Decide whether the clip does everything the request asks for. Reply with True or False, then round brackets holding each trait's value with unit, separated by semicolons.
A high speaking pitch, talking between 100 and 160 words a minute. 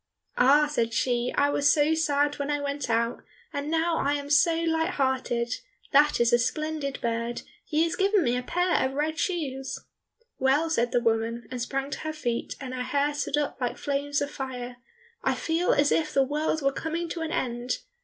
False (285 Hz; 205 wpm)